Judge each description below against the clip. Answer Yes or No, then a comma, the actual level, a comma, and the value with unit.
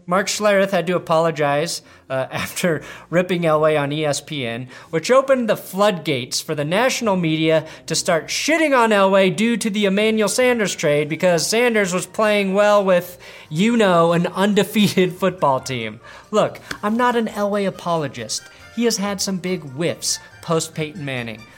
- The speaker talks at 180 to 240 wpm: No, average, 160 wpm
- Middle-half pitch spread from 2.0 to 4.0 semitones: No, average, 4.7 semitones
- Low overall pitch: No, medium, 180 Hz